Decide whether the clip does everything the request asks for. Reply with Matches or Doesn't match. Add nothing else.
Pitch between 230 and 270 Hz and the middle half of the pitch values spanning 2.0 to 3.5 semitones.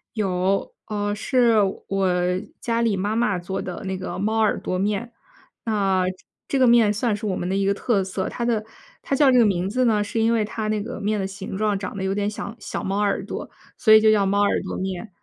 Doesn't match